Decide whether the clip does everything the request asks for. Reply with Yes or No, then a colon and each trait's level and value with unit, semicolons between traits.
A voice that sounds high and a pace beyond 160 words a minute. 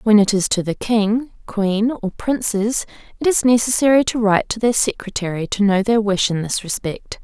Yes: high, 215 Hz; average, 200 wpm